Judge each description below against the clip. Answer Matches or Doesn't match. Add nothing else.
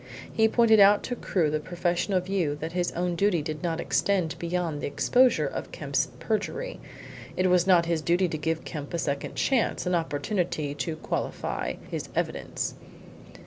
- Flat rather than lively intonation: Doesn't match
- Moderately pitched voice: Matches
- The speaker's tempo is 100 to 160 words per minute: Doesn't match